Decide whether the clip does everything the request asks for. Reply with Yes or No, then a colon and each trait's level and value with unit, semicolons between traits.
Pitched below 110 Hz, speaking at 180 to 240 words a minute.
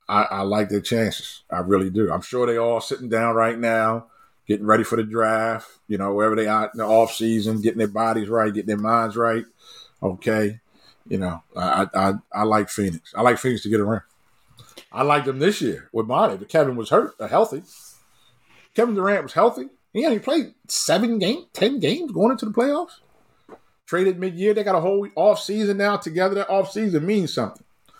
No: low, 115 Hz; fast, 205 wpm